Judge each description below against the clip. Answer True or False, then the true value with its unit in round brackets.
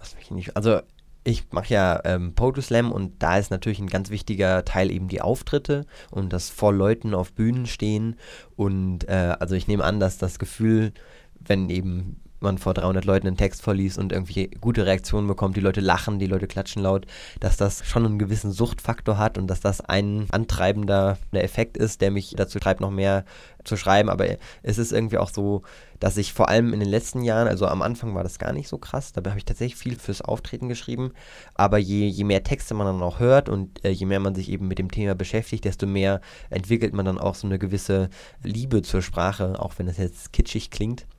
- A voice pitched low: True (100 Hz)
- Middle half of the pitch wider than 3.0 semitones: False (2.6 semitones)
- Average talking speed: False (215 wpm)